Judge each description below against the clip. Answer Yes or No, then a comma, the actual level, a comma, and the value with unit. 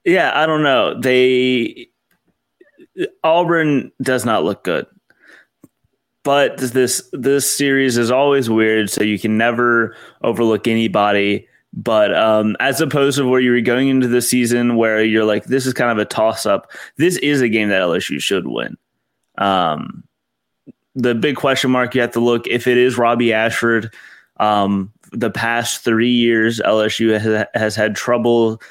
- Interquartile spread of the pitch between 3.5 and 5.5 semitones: No, average, 2.9 semitones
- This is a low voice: Yes, low, 120 Hz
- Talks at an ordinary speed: Yes, average, 160 wpm